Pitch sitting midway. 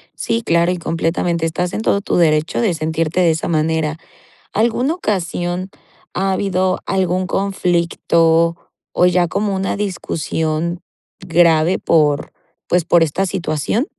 Yes: medium, 175 Hz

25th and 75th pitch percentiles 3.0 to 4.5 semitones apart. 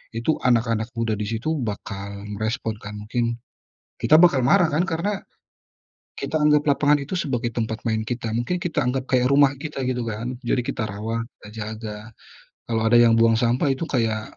Yes: average, 4.1 semitones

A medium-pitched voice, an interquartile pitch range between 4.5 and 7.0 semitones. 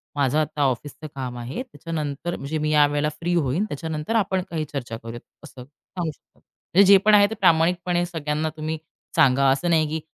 No: medium, 155 Hz; average, 3.4 semitones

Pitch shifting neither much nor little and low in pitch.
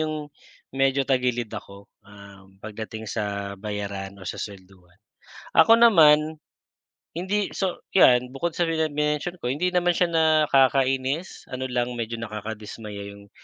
No: wide, 7.2 semitones; low, 125 Hz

